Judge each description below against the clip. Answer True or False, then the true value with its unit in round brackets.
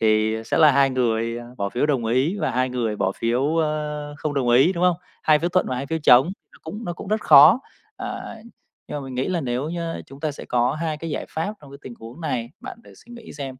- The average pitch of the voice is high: False (140 Hz)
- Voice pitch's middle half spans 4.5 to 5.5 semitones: True (4.8 semitones)